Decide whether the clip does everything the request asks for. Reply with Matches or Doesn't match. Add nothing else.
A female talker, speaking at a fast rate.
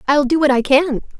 Matches